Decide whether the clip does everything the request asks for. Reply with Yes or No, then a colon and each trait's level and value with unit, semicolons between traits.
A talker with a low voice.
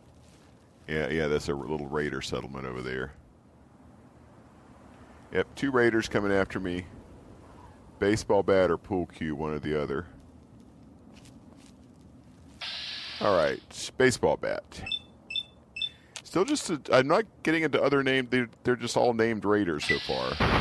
Yes: very low, 95 Hz